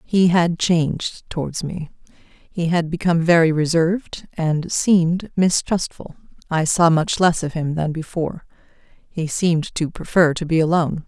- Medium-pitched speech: Yes, medium, 165 Hz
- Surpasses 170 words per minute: No, average, 150 wpm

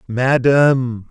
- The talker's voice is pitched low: Yes, low, 125 Hz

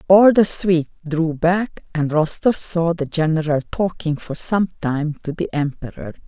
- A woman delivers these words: Yes, female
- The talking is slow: No, average, 165 wpm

